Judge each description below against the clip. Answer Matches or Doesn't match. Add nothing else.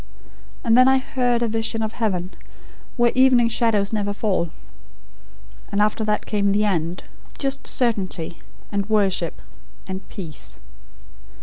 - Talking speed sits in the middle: Doesn't match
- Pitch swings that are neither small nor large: Matches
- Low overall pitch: Doesn't match